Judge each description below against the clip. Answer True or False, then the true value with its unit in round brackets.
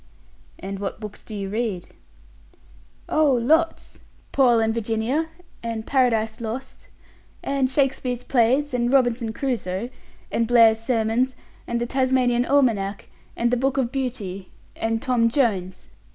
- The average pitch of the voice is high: True (240 Hz)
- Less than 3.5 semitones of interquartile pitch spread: True (2.9 semitones)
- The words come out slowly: True (130 wpm)